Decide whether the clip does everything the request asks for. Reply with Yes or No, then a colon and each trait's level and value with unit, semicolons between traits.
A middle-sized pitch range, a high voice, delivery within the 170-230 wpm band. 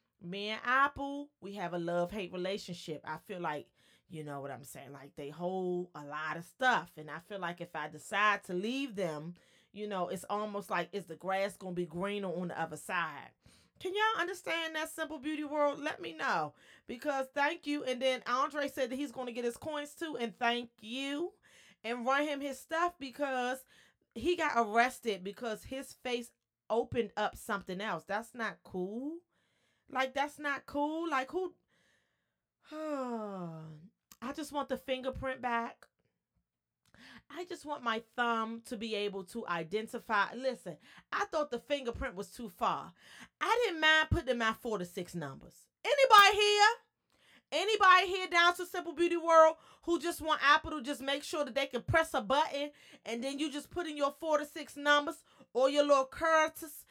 No: wide, 6.9 semitones; very high, 255 Hz; average, 185 wpm